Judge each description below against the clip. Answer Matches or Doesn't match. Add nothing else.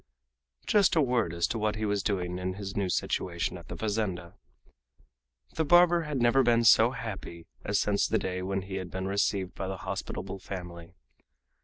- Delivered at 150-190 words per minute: Matches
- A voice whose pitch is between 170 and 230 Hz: Doesn't match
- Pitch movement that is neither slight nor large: Matches